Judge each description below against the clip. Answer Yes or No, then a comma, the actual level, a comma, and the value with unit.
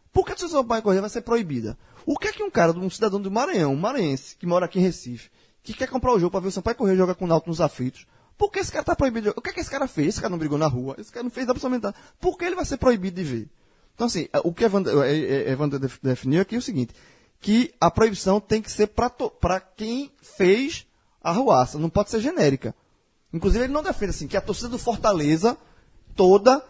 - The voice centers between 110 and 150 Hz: No, high, 200 Hz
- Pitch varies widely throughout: Yes, wide, 7.3 semitones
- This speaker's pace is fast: Yes, fast, 255 wpm